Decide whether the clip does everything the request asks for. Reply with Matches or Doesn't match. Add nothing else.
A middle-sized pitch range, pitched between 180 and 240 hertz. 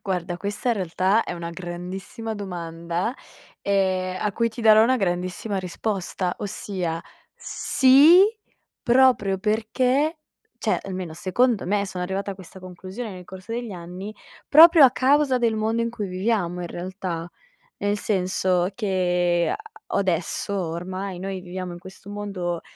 Matches